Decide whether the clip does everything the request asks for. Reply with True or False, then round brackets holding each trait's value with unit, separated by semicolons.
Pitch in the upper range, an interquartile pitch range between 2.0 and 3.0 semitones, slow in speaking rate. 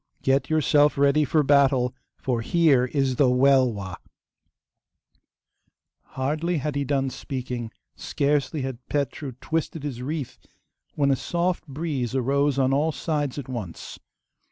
False (140 Hz; 2.5 semitones; 130 wpm)